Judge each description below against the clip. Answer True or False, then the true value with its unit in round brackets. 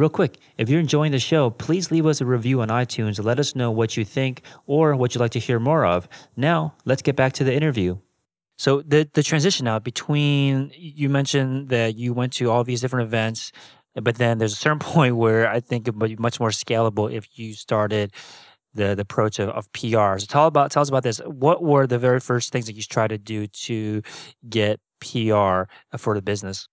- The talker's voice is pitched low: True (120 Hz)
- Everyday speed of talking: False (220 wpm)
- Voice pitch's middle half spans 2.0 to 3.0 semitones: False (4.2 semitones)